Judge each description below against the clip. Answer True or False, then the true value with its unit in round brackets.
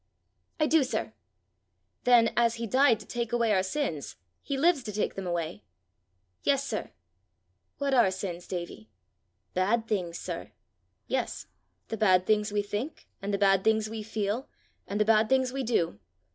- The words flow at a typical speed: True (165 wpm)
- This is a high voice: True (215 Hz)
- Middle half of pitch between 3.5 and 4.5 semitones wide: True (4.0 semitones)